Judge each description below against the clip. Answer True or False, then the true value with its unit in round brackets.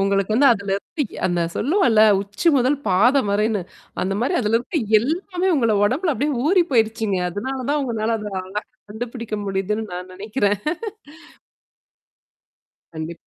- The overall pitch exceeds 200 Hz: True (220 Hz)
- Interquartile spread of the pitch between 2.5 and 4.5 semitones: False (5.1 semitones)